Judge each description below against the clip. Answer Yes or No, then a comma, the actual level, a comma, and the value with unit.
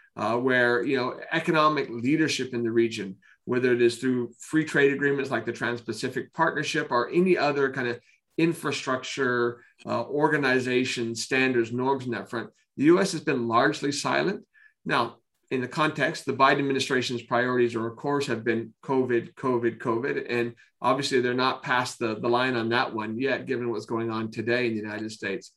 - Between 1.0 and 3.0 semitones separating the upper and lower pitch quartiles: Yes, narrow, 2.6 semitones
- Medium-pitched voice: No, low, 125 Hz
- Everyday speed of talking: Yes, average, 180 wpm